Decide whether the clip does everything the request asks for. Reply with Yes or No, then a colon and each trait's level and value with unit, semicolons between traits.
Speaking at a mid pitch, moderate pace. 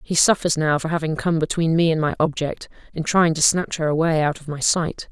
No: medium, 160 Hz; fast, 235 wpm